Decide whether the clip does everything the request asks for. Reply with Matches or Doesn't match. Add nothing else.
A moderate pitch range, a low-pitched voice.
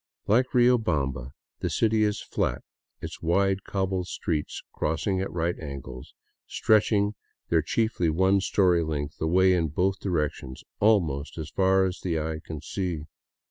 Matches